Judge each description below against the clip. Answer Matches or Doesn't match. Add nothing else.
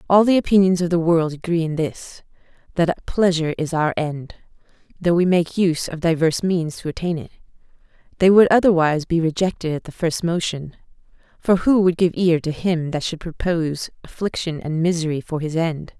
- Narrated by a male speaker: Doesn't match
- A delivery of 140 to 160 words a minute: Doesn't match